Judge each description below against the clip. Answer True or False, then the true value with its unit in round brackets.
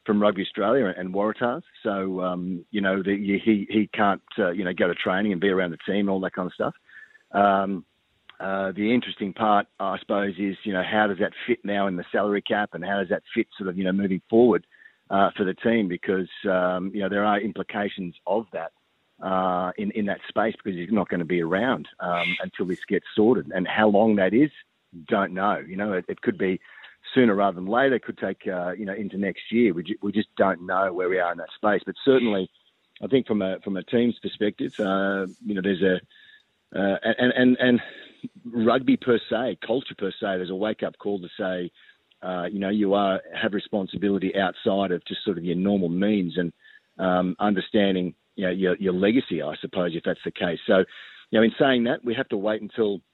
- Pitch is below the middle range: True (100 Hz)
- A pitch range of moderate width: False (2.3 semitones)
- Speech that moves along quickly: True (225 wpm)